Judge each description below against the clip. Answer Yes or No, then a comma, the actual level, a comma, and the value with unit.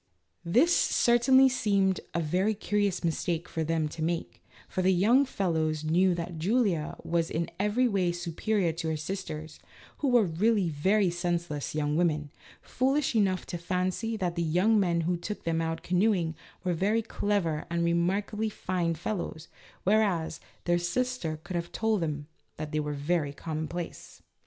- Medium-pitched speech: Yes, medium, 175 Hz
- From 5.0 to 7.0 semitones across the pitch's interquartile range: No, average, 4.1 semitones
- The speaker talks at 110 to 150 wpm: No, average, 160 wpm